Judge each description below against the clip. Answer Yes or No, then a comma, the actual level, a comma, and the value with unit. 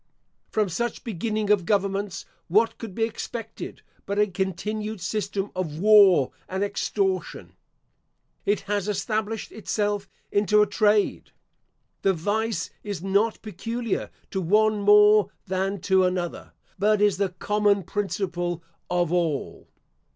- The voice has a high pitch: Yes, high, 205 Hz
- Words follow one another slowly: Yes, slow, 125 wpm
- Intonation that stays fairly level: Yes, narrow, 2.2 semitones